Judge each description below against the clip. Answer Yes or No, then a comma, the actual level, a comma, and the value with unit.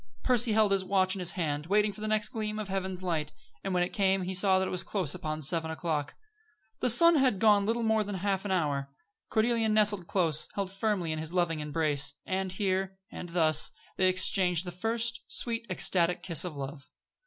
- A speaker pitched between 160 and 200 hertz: Yes, medium, 185 Hz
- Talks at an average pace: No, fast, 210 wpm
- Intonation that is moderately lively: Yes, average, 4.0 semitones